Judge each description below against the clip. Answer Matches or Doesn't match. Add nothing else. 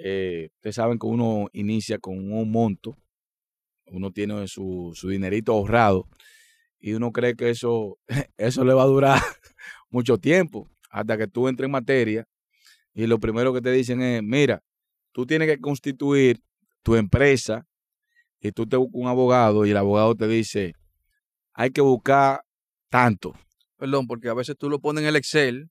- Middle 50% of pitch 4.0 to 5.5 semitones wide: Matches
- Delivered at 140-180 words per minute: Matches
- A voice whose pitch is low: Matches